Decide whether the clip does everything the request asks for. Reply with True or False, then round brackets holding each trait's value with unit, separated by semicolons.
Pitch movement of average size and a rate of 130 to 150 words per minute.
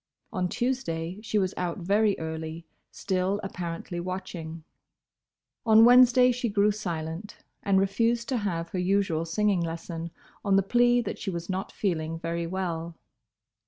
True (4.1 semitones; 145 wpm)